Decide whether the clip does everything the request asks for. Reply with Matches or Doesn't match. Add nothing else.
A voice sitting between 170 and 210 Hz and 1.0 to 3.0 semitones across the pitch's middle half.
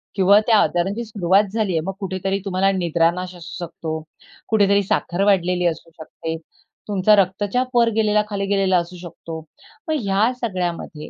Matches